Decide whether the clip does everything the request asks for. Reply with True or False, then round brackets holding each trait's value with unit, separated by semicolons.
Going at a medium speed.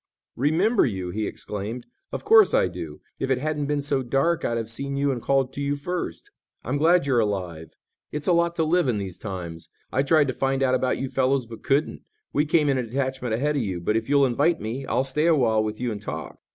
False (235 wpm)